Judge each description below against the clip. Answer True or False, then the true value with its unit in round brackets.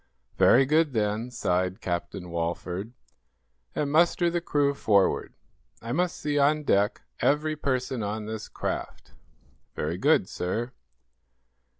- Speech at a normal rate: False (120 wpm)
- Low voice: True (120 Hz)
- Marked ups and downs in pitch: True (6.9 semitones)